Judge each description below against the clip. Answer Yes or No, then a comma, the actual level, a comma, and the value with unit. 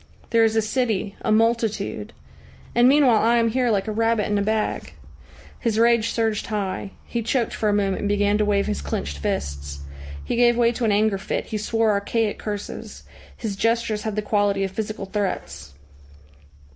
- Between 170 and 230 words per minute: Yes, average, 185 wpm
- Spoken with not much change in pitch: Yes, narrow, 2.2 semitones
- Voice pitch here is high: Yes, high, 215 Hz